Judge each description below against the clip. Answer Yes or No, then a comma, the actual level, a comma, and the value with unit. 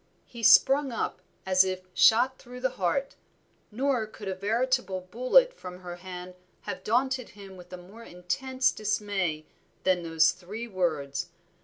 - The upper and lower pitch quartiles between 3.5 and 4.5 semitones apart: No, wide, 5.6 semitones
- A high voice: Yes, high, 200 Hz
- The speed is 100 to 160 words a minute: Yes, average, 150 wpm